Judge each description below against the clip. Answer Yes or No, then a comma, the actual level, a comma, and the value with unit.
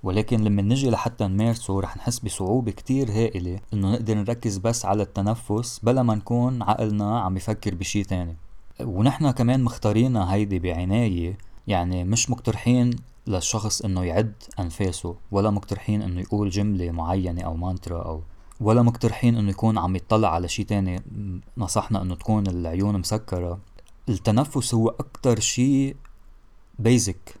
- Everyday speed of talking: No, fast, 140 wpm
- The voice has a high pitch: No, low, 105 Hz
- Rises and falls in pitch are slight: No, average, 3.7 semitones